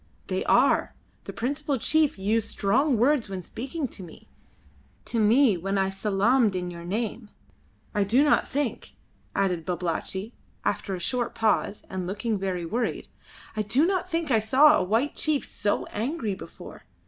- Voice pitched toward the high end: Yes, high, 220 Hz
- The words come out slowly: No, average, 160 wpm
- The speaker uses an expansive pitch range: Yes, wide, 5.7 semitones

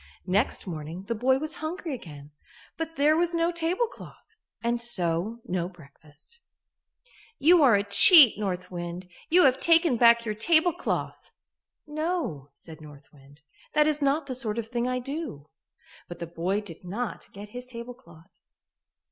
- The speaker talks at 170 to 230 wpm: No, average, 155 wpm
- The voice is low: No, high, 235 Hz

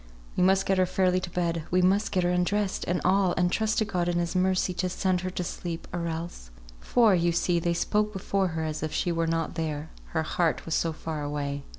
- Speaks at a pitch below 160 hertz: No, medium, 175 Hz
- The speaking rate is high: Yes, fast, 245 wpm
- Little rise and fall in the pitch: Yes, narrow, 2.3 semitones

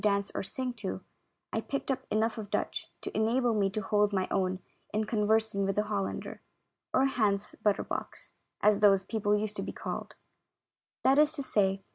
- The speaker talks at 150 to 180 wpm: No, average, 190 wpm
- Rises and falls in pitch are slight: Yes, narrow, 1.9 semitones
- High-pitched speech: Yes, high, 210 Hz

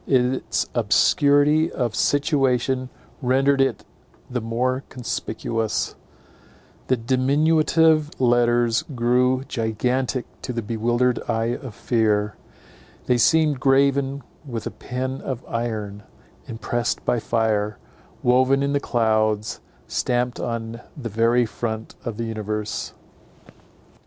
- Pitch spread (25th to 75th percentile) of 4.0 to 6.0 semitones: No, average, 2.8 semitones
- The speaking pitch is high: No, low, 120 Hz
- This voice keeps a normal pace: No, slow, 105 wpm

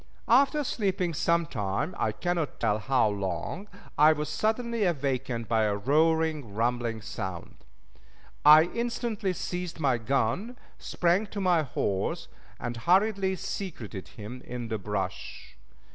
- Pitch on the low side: No, medium, 150 Hz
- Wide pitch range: Yes, wide, 8.6 semitones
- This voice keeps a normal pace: No, slow, 130 wpm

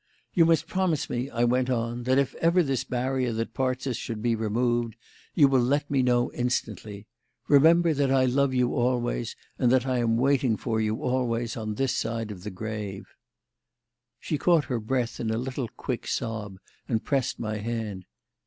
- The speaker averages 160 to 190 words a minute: Yes, average, 185 wpm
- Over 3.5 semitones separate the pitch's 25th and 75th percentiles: No, average, 2.8 semitones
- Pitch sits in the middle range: No, low, 125 Hz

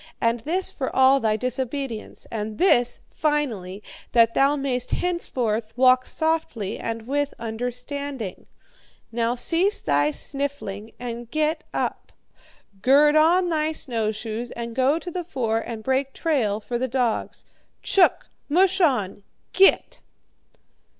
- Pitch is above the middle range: Yes, very high, 255 Hz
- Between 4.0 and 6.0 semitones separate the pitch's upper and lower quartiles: Yes, average, 4.7 semitones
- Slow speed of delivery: Yes, slow, 125 wpm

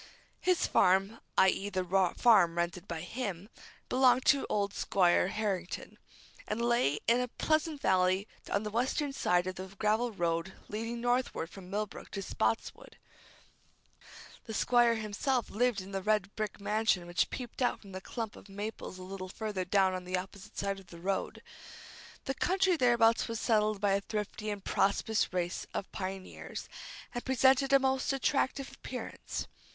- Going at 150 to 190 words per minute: Yes, average, 160 wpm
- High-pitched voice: Yes, high, 210 Hz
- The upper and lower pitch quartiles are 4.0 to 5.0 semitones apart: Yes, average, 4.3 semitones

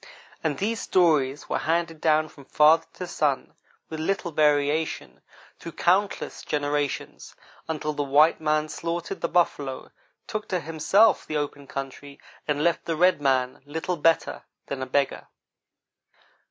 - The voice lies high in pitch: No, medium, 155 Hz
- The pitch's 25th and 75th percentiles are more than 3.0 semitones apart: No, average, 2.7 semitones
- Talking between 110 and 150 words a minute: Yes, average, 140 wpm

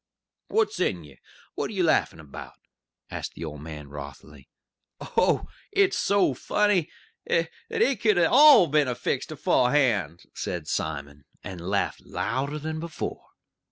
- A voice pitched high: No, low, 125 Hz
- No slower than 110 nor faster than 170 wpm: Yes, average, 140 wpm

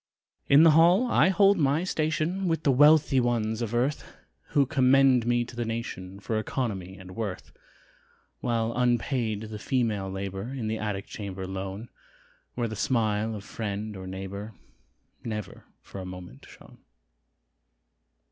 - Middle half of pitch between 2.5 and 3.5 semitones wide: No, average, 5.2 semitones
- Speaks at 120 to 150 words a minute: Yes, average, 145 wpm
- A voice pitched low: Yes, low, 115 Hz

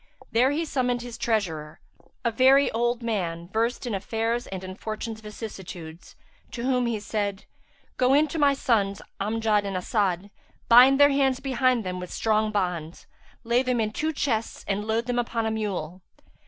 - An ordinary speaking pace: Yes, average, 170 wpm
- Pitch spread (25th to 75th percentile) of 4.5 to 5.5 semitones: No, average, 3.9 semitones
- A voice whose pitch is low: No, high, 225 Hz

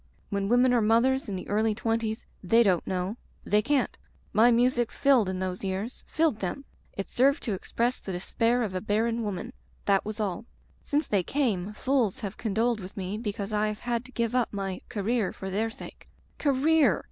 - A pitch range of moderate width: Yes, average, 3.7 semitones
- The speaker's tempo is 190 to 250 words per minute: Yes, average, 195 wpm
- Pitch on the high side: Yes, high, 220 Hz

